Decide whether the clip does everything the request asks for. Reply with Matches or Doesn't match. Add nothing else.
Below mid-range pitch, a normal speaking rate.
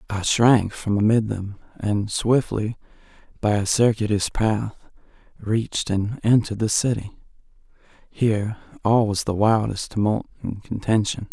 Doesn't match